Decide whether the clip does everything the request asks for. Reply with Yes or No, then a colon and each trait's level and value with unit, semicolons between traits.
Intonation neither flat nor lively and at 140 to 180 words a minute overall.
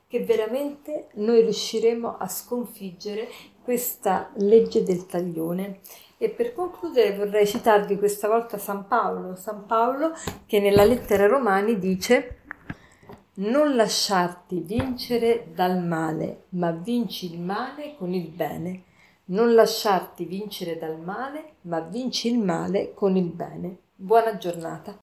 No: average, 4.1 semitones; average, 125 wpm